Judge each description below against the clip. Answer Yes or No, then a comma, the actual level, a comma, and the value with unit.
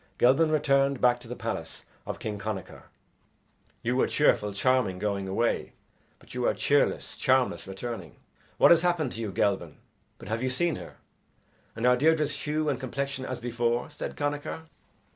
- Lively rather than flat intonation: No, average, 4.6 semitones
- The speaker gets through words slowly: No, average, 165 wpm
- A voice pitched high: No, low, 125 Hz